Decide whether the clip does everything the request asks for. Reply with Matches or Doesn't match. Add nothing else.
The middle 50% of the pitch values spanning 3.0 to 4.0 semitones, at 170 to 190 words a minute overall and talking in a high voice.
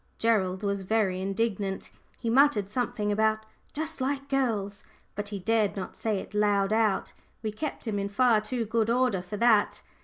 Doesn't match